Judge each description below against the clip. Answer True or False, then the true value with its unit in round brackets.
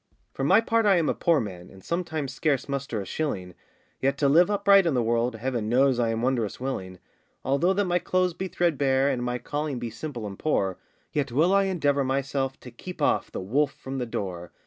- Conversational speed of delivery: False (215 wpm)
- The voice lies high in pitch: False (135 Hz)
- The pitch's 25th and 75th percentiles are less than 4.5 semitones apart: False (5.6 semitones)